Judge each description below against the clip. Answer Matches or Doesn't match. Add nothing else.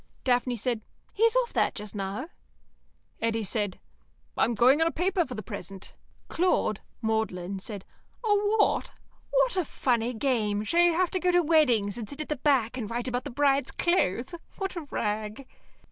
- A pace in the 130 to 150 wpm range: Doesn't match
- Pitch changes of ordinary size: Doesn't match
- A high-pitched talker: Matches